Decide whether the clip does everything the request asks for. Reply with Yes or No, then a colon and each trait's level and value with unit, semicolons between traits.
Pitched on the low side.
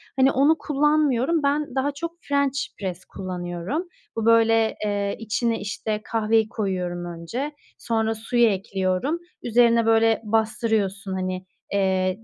No: high, 225 Hz